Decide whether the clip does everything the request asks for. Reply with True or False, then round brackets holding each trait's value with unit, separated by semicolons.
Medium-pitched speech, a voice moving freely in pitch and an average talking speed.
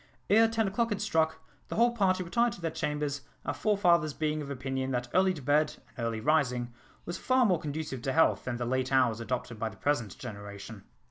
False (150 Hz; 7.0 semitones; 210 wpm)